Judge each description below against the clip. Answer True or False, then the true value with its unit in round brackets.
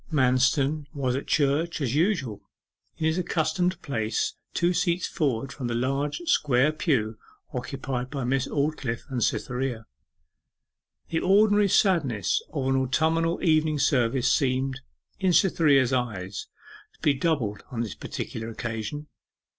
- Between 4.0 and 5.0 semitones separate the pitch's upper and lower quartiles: True (4.4 semitones)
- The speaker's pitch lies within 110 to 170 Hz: True (135 Hz)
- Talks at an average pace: False (130 wpm)